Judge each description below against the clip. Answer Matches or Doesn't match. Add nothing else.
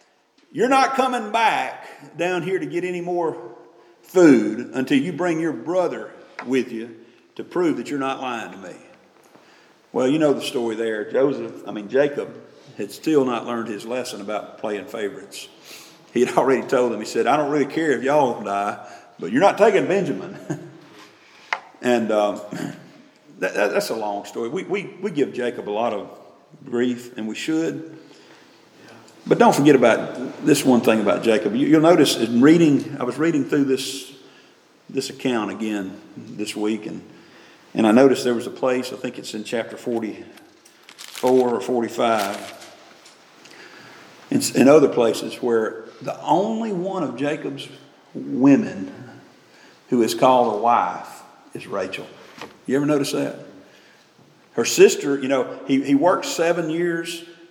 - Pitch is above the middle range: Doesn't match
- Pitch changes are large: Matches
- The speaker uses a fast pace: Doesn't match